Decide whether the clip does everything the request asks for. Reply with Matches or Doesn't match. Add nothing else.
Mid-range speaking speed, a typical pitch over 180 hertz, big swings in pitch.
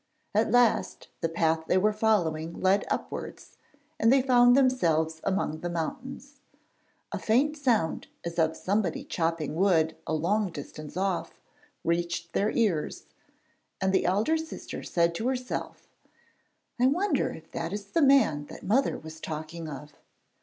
Matches